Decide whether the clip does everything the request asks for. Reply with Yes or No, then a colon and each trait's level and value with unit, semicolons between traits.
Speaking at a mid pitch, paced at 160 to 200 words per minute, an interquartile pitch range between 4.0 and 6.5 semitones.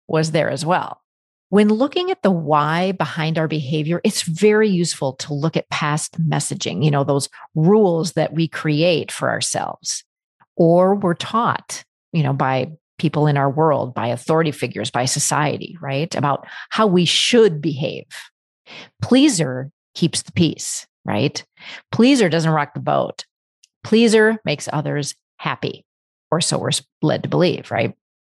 No: medium, 160 Hz; average, 150 wpm; average, 4.4 semitones